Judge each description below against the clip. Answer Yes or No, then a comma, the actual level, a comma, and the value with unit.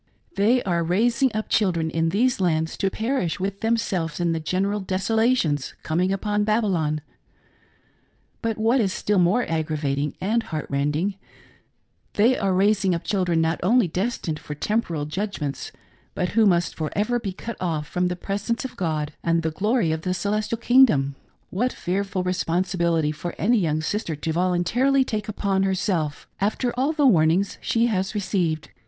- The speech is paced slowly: No, average, 170 wpm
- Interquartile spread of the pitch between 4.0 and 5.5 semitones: Yes, average, 4.8 semitones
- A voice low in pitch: No, high, 190 Hz